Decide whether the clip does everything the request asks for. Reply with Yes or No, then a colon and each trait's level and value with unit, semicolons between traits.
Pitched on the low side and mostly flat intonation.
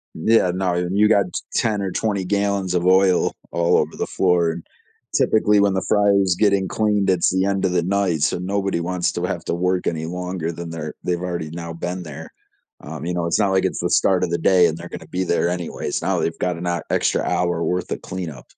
Yes: very low, 90 Hz; narrow, 2.1 semitones